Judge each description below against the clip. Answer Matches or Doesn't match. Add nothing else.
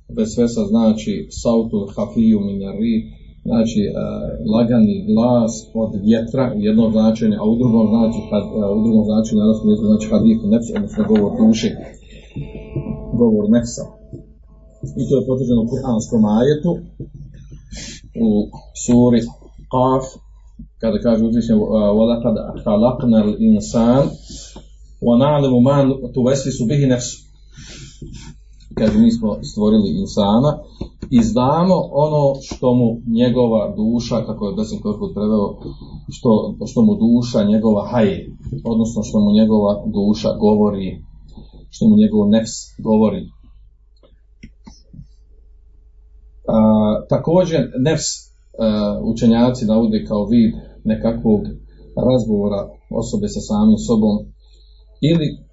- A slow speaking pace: Matches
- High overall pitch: Doesn't match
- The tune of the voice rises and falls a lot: Matches